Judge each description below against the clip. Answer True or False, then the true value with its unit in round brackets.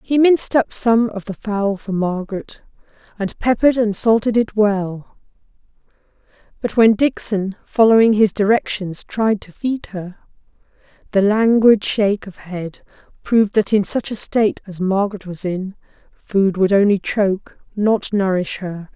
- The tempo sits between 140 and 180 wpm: True (150 wpm)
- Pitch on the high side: True (205 Hz)